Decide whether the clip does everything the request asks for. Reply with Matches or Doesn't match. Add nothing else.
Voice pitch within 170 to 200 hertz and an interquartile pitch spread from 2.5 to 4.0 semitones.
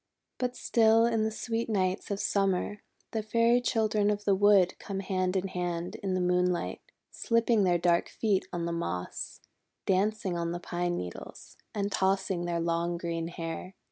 Matches